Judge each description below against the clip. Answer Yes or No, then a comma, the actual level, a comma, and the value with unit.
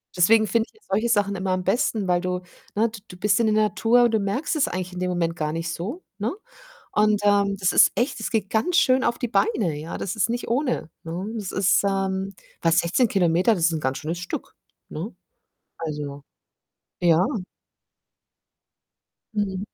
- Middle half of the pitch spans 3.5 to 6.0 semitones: Yes, average, 3.9 semitones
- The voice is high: Yes, high, 195 Hz